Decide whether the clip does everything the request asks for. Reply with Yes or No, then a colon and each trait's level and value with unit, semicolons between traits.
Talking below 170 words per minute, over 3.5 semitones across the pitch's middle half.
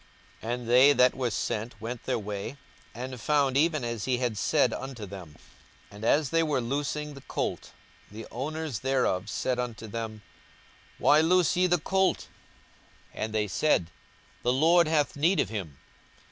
No: average, 175 wpm; average, 5.2 semitones